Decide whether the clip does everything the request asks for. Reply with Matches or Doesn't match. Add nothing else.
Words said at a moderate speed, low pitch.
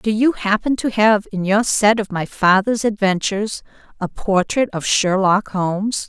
Doesn't match